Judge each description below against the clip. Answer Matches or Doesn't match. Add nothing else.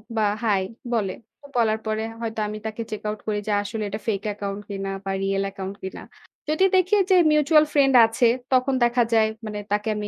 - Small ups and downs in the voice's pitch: Doesn't match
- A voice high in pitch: Matches